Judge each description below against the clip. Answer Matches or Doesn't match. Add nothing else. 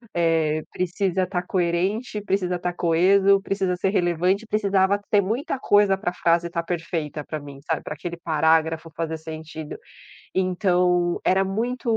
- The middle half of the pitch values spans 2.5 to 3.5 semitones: Matches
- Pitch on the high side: Doesn't match